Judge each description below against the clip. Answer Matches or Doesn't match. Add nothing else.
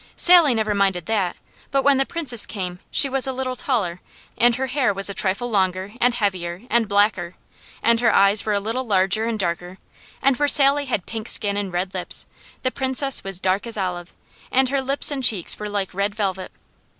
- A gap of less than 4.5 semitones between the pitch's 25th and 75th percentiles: Doesn't match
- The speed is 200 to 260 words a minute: Matches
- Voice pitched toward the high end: Matches